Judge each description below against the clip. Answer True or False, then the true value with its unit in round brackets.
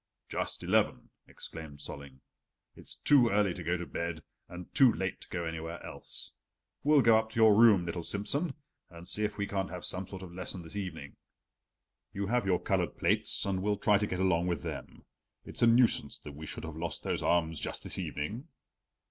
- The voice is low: True (95 Hz)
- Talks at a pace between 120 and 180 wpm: False (205 wpm)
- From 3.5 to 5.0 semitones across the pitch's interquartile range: True (3.8 semitones)